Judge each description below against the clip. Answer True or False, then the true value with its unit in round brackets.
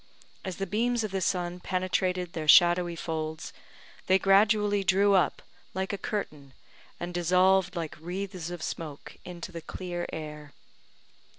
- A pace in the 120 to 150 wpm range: True (140 wpm)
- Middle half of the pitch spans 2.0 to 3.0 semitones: True (2.4 semitones)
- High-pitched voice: False (180 Hz)